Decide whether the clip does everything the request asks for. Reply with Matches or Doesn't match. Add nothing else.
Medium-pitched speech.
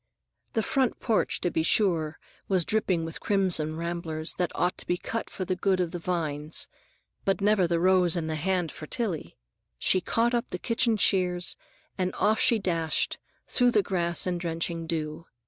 Matches